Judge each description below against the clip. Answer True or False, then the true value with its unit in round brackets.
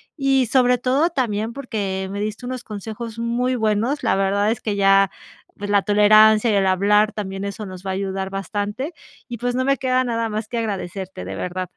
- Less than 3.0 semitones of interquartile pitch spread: False (3.7 semitones)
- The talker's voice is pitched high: True (215 Hz)